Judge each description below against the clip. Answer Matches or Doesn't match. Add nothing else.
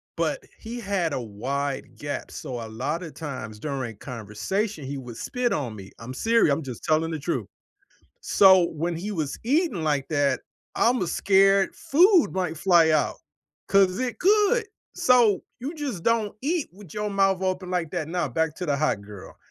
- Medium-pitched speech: Matches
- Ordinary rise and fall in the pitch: Doesn't match